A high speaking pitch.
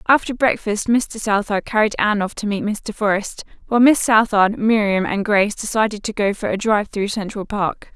Yes: high, 210 Hz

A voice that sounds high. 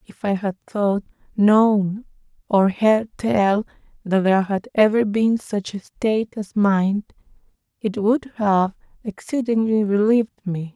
Yes: high, 210 Hz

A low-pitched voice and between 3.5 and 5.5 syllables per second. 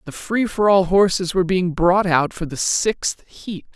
No: medium, 185 Hz; 4.3 syllables/s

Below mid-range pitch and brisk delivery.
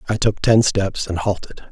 Yes: low, 100 Hz; fast, 210 wpm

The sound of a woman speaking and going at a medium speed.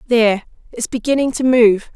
No: female; slow, 125 wpm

